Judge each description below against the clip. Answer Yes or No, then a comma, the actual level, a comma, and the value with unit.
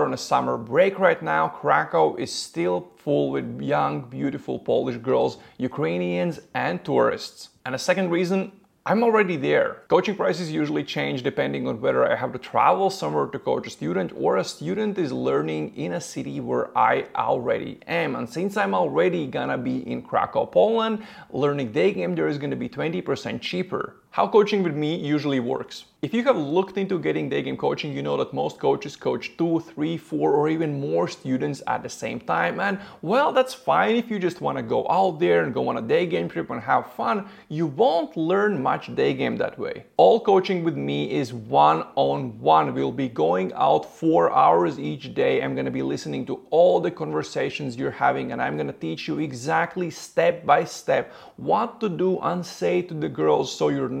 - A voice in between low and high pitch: Yes, medium, 165 Hz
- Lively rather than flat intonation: Yes, wide, 8.8 semitones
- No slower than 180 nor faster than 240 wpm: Yes, average, 200 wpm